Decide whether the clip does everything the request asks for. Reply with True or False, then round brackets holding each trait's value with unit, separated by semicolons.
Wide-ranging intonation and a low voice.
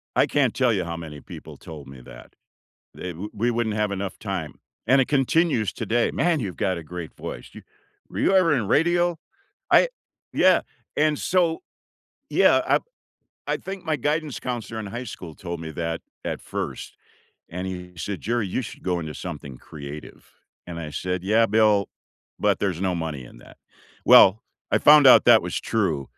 True (6.9 semitones; 100 Hz)